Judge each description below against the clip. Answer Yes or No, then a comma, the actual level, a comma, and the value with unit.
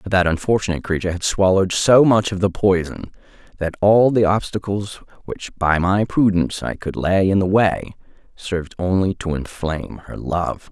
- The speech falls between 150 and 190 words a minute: Yes, average, 175 wpm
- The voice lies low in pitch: Yes, very low, 95 Hz